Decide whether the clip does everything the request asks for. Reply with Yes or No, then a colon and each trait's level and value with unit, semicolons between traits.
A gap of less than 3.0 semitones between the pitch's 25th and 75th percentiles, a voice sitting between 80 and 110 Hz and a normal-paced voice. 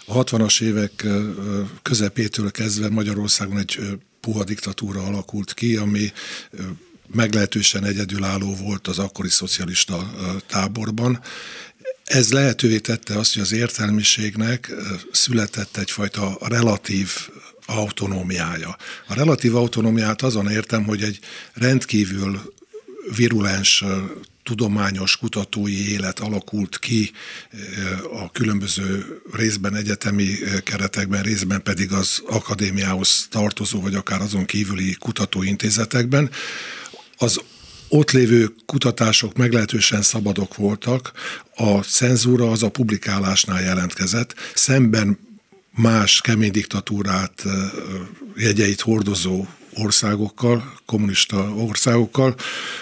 No: narrow, 2.5 semitones; low, 105 Hz; slow, 90 wpm